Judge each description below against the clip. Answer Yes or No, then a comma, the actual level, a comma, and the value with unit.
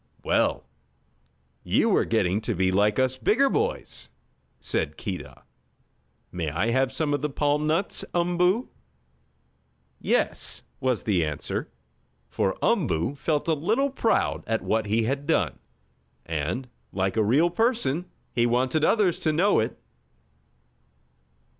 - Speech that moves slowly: Yes, slow, 130 wpm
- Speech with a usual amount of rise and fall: No, wide, 8.5 semitones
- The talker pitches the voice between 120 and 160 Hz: Yes, low, 135 Hz